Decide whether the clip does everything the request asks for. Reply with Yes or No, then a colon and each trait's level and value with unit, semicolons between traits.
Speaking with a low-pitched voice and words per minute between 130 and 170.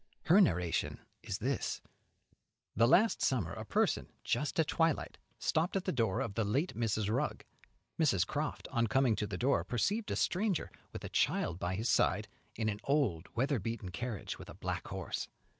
No: low, 120 Hz; average, 180 wpm